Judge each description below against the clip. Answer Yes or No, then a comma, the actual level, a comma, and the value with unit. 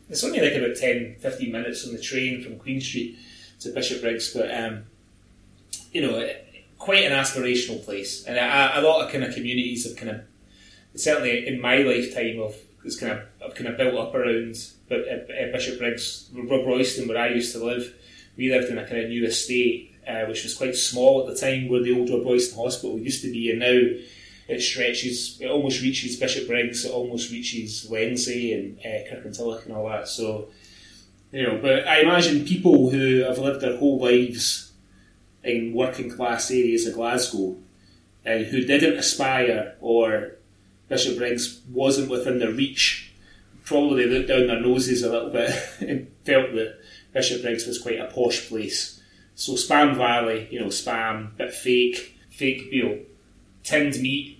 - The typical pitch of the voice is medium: No, low, 120 Hz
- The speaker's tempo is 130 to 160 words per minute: No, average, 180 wpm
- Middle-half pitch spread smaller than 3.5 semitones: Yes, narrow, 2.4 semitones